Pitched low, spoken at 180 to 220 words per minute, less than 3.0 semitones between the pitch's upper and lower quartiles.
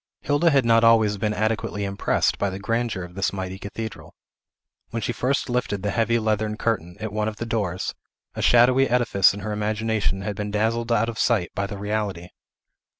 Yes: low, 110 Hz; average, 195 wpm; narrow, 2.5 semitones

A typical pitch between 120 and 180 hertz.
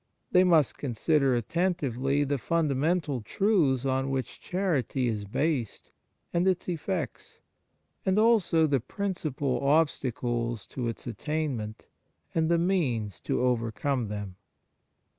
Yes: medium, 140 Hz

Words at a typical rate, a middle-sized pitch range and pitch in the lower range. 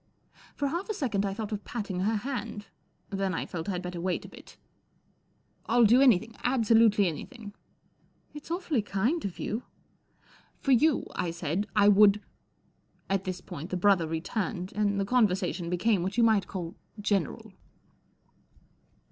No: average, 170 wpm; average, 3.9 semitones; high, 205 Hz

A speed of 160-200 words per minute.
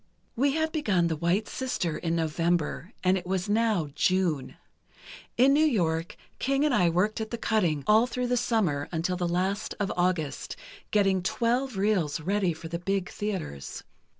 Yes: average, 170 wpm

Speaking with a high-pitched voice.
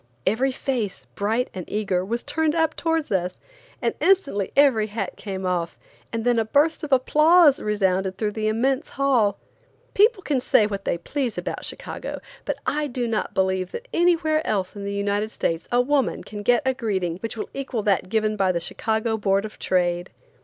Yes: high, 220 Hz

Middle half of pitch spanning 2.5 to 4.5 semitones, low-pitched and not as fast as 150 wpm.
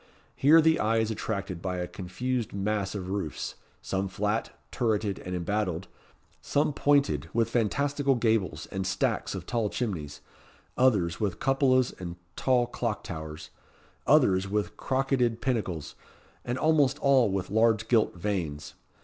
No: average, 5.1 semitones; low, 105 Hz; average, 140 wpm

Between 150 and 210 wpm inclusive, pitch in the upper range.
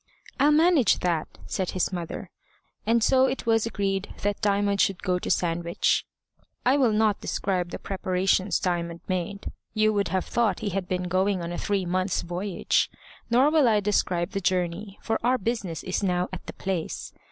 Yes: average, 180 wpm; high, 195 Hz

